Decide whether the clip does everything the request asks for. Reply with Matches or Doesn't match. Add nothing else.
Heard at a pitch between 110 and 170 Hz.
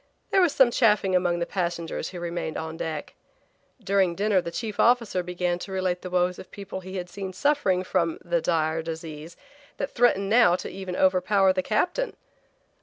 Doesn't match